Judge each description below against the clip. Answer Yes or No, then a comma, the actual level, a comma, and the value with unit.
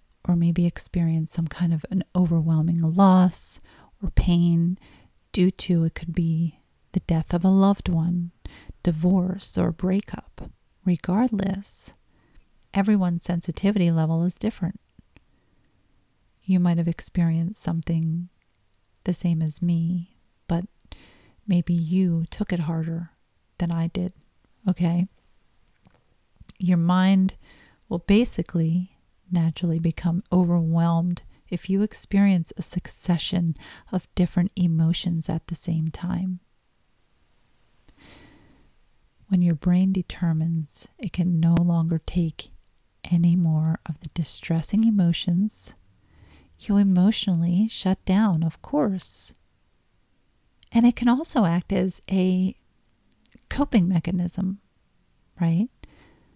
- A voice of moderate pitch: Yes, medium, 175 Hz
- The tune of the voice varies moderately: No, narrow, 2.1 semitones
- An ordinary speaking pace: No, slow, 105 wpm